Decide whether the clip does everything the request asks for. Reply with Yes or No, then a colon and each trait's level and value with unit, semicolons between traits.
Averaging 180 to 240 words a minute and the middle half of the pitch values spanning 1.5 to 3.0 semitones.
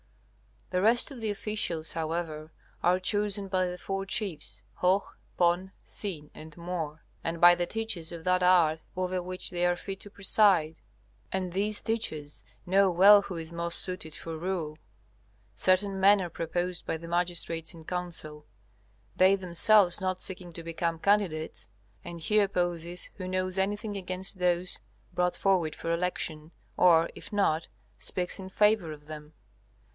No: average, 155 wpm; narrow, 2.6 semitones